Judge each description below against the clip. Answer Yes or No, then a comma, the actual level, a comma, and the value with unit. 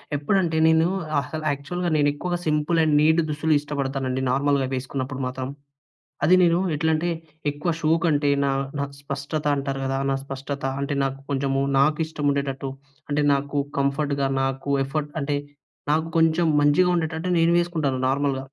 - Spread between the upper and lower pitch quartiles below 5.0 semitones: Yes, narrow, 2.6 semitones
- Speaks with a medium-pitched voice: Yes, medium, 145 Hz